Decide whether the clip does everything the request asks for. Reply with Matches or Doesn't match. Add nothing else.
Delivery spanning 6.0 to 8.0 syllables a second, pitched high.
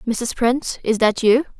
Doesn't match